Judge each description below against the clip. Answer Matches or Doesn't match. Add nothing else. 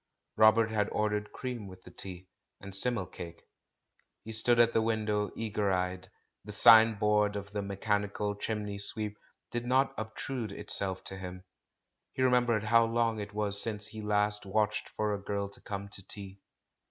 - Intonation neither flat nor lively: Doesn't match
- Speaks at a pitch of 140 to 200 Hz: Doesn't match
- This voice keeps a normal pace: Matches